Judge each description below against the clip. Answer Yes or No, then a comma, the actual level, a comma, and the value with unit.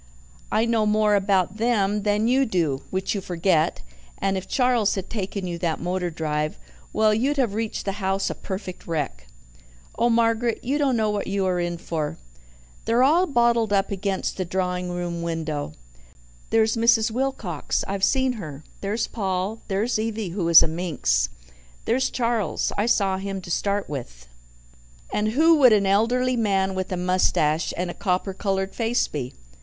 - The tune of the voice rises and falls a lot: No, average, 4.2 semitones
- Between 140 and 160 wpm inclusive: No, average, 170 wpm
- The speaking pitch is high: Yes, high, 195 Hz